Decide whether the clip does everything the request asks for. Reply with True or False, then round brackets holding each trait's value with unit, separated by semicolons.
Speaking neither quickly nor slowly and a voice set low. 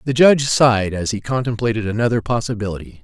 True (160 wpm; 110 Hz)